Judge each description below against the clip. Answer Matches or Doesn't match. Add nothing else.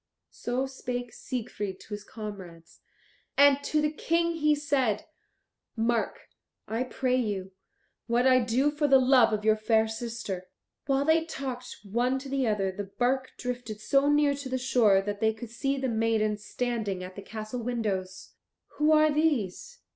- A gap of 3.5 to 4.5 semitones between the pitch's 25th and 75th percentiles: Matches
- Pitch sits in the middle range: Doesn't match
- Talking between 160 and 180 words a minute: Matches